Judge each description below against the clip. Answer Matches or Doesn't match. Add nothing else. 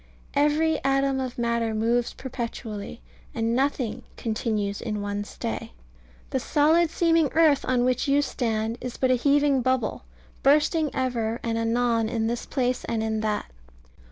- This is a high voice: Matches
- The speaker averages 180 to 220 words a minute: Doesn't match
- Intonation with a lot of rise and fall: Doesn't match